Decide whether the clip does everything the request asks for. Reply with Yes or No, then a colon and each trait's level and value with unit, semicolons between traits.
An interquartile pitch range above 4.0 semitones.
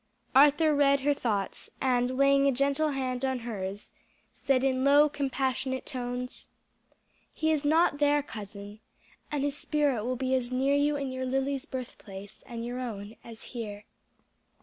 No: average, 2.7 semitones